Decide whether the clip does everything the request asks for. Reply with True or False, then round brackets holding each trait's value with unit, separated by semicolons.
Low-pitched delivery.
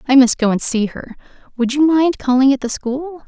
False (265 Hz)